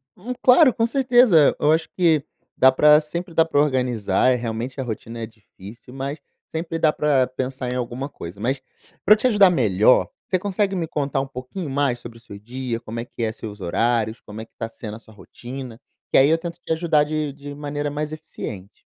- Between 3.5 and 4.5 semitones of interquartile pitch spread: No, average, 5.3 semitones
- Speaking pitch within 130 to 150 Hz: Yes, low, 135 Hz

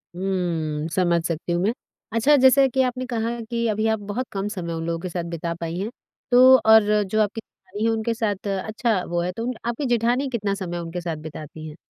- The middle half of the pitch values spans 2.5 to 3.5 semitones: No, average, 5.2 semitones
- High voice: Yes, high, 205 Hz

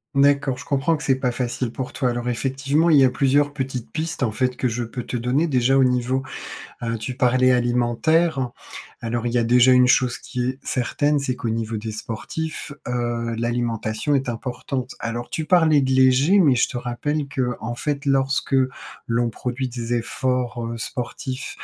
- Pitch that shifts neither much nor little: No, narrow, 2.3 semitones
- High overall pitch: No, low, 125 Hz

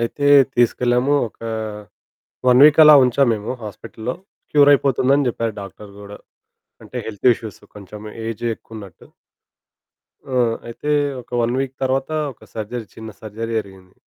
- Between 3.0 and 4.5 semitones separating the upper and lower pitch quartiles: Yes, average, 3.7 semitones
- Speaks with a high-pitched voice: No, low, 115 Hz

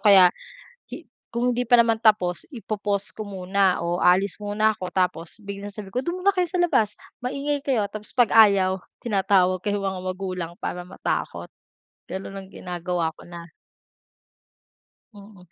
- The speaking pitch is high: Yes, high, 200 Hz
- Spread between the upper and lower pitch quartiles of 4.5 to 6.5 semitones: No, average, 3.0 semitones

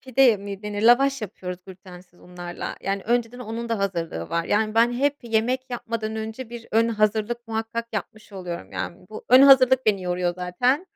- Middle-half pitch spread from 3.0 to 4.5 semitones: Yes, average, 4.0 semitones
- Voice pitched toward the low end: No, high, 220 Hz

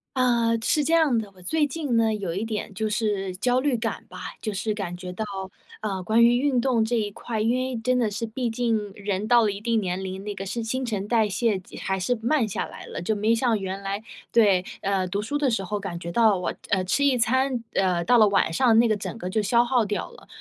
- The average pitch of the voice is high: Yes, high, 220 Hz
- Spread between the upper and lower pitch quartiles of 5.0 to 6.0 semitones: No, average, 3.4 semitones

